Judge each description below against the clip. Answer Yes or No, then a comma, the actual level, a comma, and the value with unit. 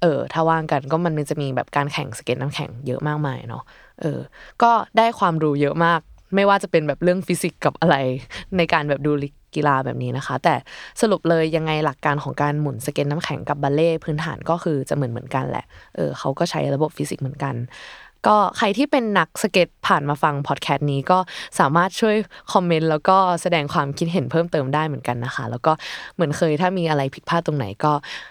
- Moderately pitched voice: Yes, medium, 155 Hz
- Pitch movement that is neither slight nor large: Yes, average, 3.4 semitones